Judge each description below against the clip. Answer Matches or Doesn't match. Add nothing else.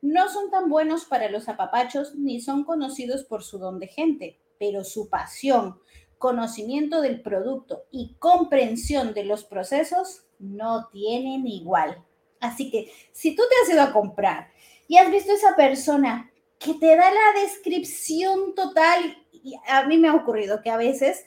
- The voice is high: Matches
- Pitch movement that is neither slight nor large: Doesn't match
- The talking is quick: Doesn't match